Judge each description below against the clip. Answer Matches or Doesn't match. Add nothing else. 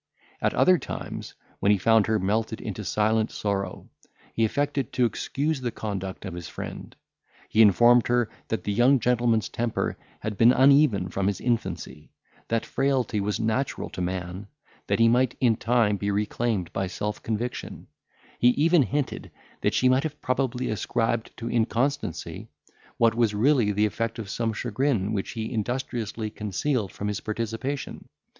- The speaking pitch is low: Matches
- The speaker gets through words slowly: Doesn't match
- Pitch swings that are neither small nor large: Matches